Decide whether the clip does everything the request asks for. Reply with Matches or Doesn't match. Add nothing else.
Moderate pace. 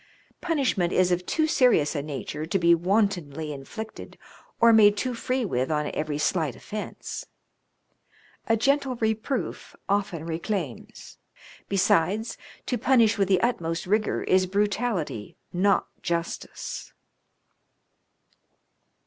Doesn't match